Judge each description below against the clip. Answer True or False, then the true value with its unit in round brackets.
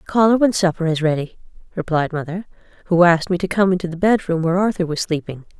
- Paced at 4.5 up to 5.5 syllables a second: False (6.4 syllables/s)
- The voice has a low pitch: False (175 Hz)